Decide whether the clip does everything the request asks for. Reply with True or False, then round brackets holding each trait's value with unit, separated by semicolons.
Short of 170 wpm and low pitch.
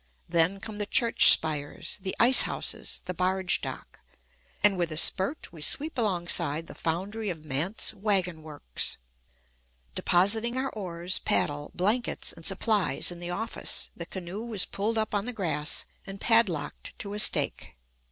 False (155 wpm; 190 Hz)